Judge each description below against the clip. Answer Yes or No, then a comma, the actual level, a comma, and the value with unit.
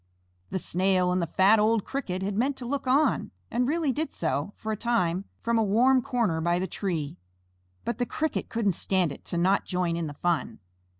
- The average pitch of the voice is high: Yes, high, 200 Hz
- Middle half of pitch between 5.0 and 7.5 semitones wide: Yes, wide, 5.5 semitones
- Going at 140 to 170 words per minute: No, fast, 205 wpm